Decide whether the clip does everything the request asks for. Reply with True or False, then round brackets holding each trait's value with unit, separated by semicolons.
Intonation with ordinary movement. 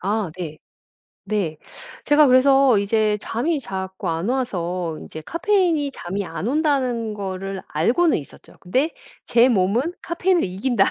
False (6.6 semitones)